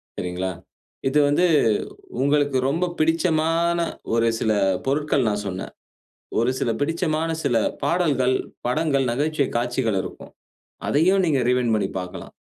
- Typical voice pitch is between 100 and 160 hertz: Yes, medium, 140 Hz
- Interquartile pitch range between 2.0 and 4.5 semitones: No, average, 5.1 semitones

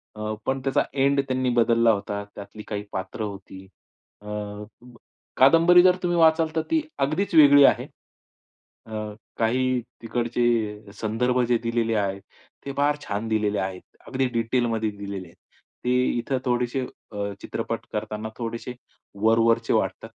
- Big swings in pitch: No, average, 3.9 semitones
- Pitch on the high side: No, low, 115 Hz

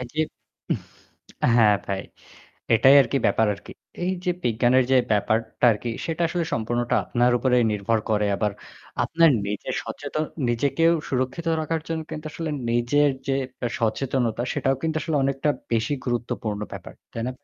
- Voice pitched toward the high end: No, low, 125 Hz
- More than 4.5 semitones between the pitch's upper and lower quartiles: Yes, average, 4.9 semitones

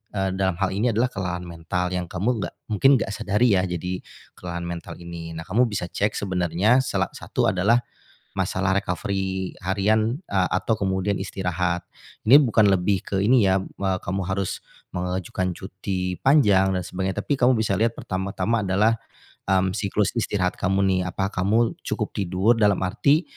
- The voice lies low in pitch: Yes, very low, 95 Hz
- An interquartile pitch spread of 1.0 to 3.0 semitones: Yes, narrow, 2.4 semitones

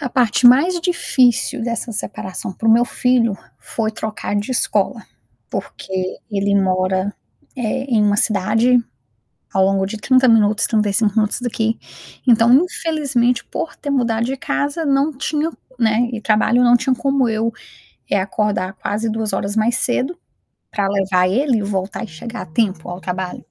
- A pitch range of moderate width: Yes, average, 3.7 semitones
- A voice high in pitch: Yes, high, 225 Hz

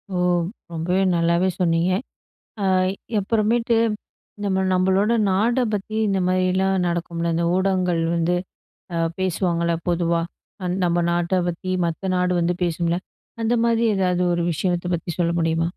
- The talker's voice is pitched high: No, medium, 180 Hz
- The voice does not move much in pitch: Yes, narrow, 2.0 semitones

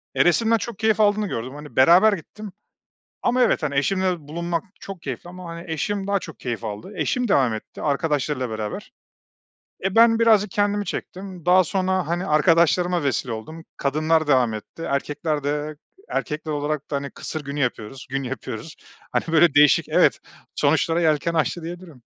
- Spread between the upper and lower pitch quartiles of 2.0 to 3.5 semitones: No, average, 4.9 semitones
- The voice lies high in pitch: No, medium, 160 Hz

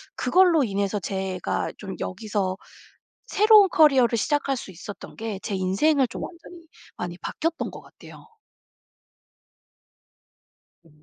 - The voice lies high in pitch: Yes, high, 225 Hz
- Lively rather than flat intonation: Yes, wide, 8.6 semitones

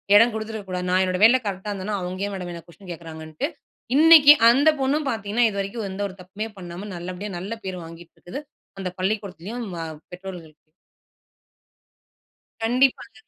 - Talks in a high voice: Yes, high, 195 Hz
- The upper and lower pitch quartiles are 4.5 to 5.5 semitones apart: No, average, 3.9 semitones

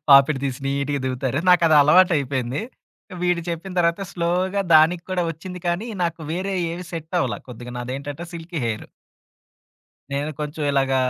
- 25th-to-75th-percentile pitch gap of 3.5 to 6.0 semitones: Yes, average, 4.1 semitones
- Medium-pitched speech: Yes, medium, 160 Hz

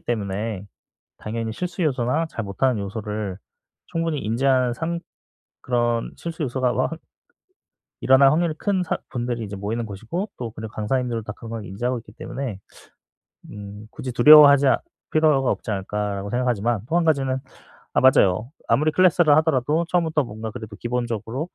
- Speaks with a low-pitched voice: Yes, low, 120 Hz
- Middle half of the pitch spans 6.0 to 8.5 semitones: No, wide, 5.5 semitones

